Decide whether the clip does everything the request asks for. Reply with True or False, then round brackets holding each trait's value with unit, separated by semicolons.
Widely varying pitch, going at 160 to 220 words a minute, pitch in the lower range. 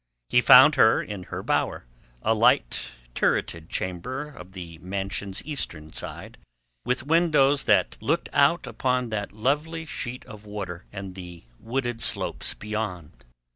False (6.7 semitones; 135 wpm; 110 Hz)